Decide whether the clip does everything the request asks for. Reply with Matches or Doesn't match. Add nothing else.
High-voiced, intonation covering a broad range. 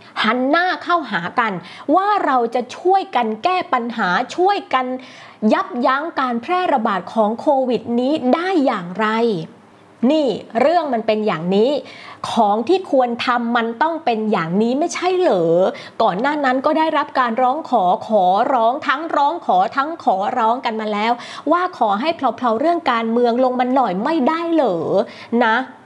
Matches